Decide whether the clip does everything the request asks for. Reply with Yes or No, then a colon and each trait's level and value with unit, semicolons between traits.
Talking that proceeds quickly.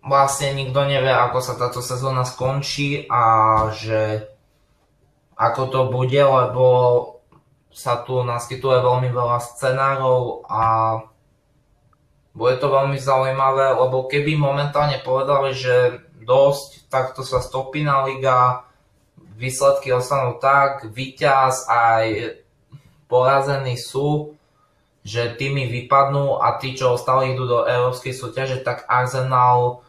No: slow, 110 wpm